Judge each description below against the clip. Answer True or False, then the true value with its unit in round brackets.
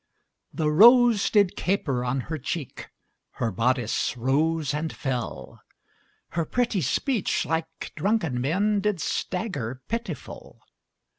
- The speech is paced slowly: True (115 wpm)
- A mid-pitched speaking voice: True (160 Hz)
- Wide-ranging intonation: True (7.5 semitones)